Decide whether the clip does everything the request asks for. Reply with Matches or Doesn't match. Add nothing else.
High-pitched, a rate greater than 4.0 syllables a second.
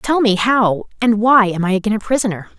Matches